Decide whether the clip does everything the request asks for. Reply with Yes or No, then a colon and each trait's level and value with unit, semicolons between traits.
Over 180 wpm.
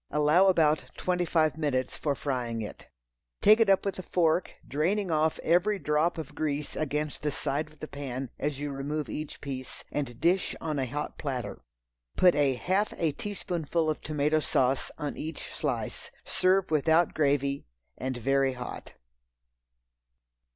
No: average, 160 wpm